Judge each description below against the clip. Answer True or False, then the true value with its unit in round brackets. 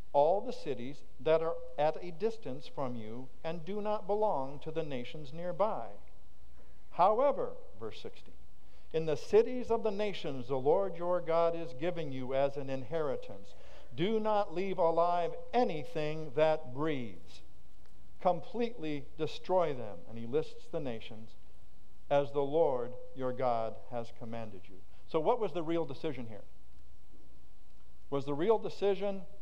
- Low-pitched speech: False (155 Hz)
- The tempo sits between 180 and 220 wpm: False (145 wpm)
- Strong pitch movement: True (6.5 semitones)